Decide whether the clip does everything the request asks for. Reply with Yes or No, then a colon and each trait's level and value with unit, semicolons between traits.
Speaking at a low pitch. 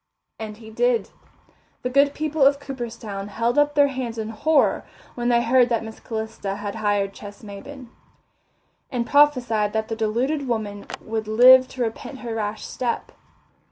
No: high, 235 Hz